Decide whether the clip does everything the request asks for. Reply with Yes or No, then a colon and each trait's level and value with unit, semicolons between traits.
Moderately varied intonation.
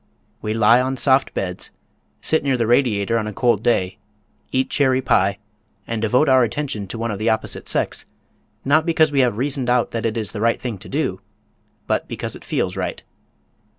Yes: average, 3.5 semitones